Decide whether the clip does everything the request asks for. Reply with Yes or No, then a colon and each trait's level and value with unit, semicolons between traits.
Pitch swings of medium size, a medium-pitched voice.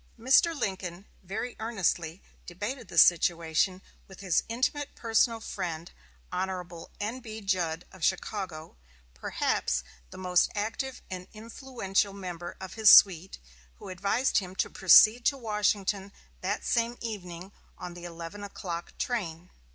No: average, 4.0 semitones; high, 195 Hz